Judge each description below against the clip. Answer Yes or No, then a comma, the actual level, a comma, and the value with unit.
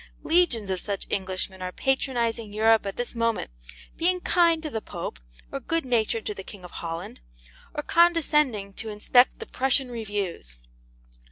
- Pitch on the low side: No, high, 225 Hz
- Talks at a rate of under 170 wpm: Yes, average, 160 wpm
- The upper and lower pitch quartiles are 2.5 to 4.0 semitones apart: No, average, 5.3 semitones